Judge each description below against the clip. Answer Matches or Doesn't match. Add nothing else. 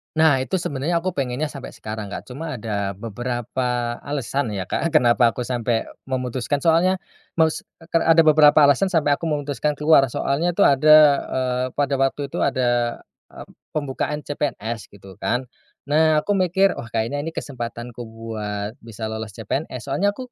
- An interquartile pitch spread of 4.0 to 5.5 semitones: Matches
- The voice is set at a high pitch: Doesn't match